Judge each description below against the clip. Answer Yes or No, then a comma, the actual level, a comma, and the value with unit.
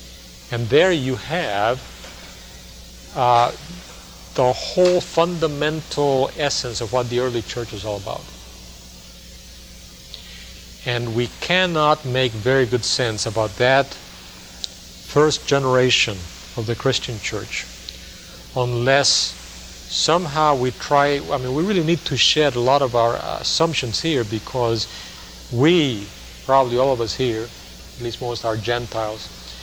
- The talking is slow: Yes, slow, 125 wpm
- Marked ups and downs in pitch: Yes, wide, 7.0 semitones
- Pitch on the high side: No, low, 120 Hz